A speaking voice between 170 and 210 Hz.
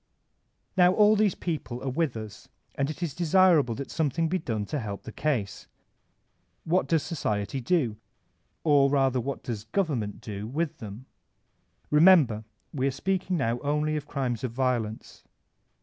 No: medium, 140 Hz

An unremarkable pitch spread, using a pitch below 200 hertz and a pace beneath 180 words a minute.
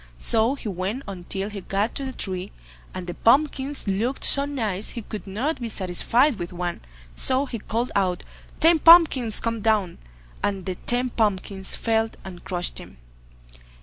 No: average, 5.0 semitones; high, 215 Hz; average, 170 wpm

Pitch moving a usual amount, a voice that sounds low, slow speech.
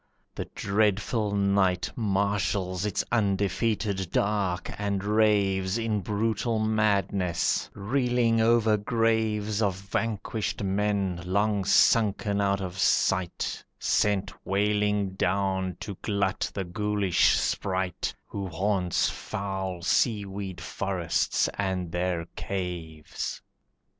No: narrow, 2.0 semitones; low, 100 Hz; slow, 100 wpm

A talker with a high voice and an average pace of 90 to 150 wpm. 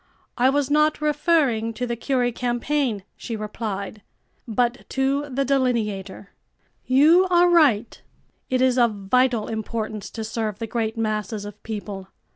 Yes: high, 235 Hz; average, 140 wpm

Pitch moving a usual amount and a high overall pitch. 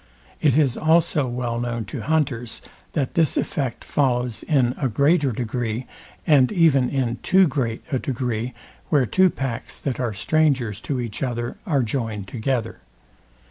No: average, 3.5 semitones; low, 130 Hz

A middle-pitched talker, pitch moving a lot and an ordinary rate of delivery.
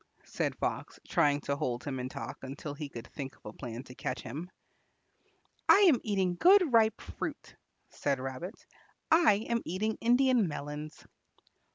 Yes: medium, 150 Hz; wide, 8.9 semitones; average, 160 wpm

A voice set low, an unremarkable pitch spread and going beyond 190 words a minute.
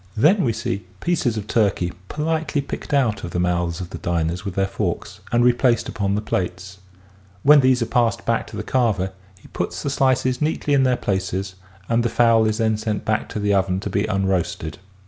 Yes: low, 110 Hz; average, 4.6 semitones; fast, 205 wpm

